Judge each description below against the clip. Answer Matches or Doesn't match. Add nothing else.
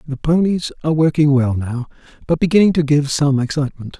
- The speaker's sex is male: Matches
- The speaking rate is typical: Matches